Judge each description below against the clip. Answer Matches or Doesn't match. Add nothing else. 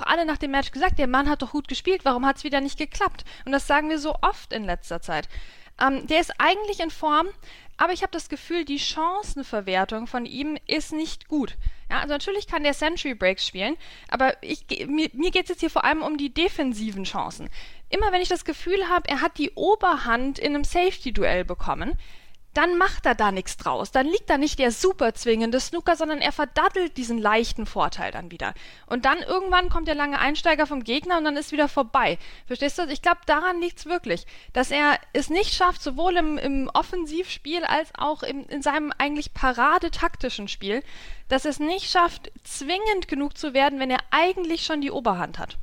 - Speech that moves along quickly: Matches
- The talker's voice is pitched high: Matches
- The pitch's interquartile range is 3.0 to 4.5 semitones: Matches